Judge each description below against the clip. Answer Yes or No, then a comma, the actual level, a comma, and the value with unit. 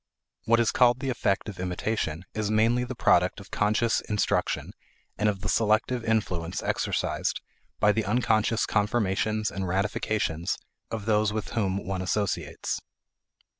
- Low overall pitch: Yes, low, 105 Hz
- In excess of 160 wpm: No, average, 140 wpm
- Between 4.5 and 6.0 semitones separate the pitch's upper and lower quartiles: No, narrow, 2.6 semitones